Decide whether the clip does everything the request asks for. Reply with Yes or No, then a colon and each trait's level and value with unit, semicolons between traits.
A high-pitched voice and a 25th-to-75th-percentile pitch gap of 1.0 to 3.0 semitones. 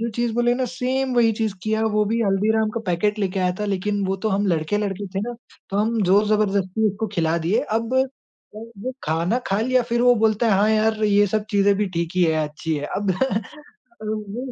Yes: high, 210 Hz; narrow, 2.6 semitones